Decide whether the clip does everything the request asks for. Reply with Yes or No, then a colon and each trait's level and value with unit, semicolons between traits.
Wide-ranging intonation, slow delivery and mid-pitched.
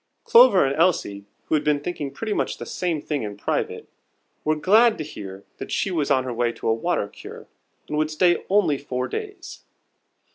No: wide, 6.0 semitones; average, 195 wpm; medium, 150 Hz